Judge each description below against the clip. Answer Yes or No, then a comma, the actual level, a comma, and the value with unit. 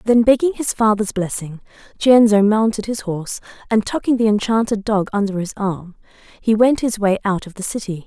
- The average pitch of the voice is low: No, high, 210 Hz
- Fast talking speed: No, average, 185 wpm